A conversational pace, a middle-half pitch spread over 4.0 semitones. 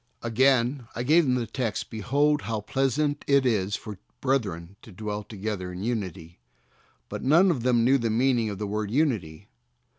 Yes: average, 175 wpm; average, 4.6 semitones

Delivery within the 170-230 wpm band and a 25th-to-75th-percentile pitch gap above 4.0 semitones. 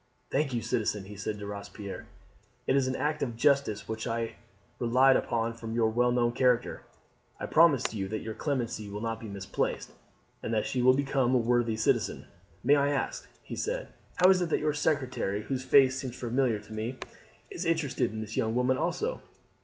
No: average, 195 wpm; average, 3.7 semitones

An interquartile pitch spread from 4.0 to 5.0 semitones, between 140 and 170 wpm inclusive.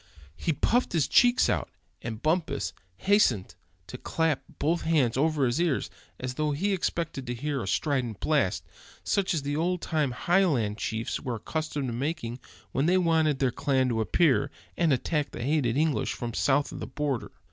No: average, 4.6 semitones; average, 180 wpm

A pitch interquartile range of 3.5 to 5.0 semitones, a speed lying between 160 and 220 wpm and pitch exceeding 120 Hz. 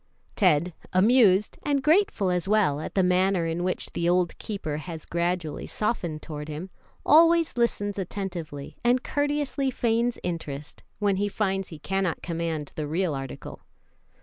No: average, 4.7 semitones; average, 150 wpm; medium, 185 Hz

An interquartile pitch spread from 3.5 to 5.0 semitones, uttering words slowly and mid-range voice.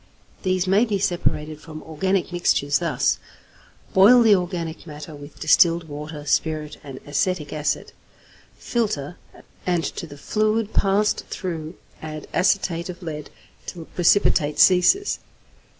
Yes: average, 3.9 semitones; slow, 125 wpm; medium, 170 Hz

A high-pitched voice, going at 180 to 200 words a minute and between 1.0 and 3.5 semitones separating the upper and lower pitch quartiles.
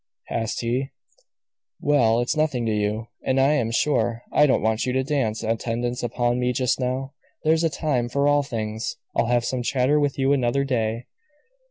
No: low, 125 Hz; average, 185 wpm; average, 3.1 semitones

